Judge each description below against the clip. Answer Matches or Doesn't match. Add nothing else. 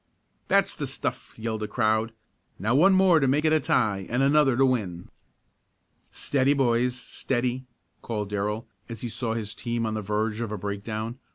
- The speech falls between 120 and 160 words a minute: Doesn't match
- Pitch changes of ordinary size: Matches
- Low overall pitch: Matches